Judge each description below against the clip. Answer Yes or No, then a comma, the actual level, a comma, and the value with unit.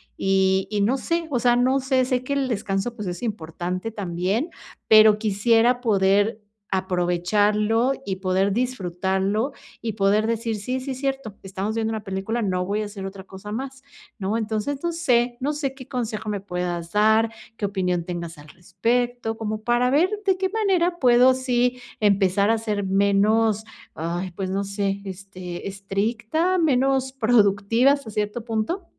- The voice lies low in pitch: No, high, 215 Hz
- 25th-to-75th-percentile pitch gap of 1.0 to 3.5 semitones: No, average, 4.3 semitones